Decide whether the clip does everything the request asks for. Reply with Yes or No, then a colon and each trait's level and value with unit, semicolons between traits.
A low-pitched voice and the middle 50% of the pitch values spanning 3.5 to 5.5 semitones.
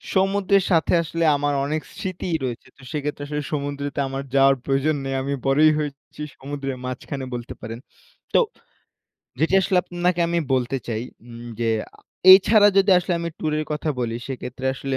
No: medium, 145 Hz; average, 3.9 semitones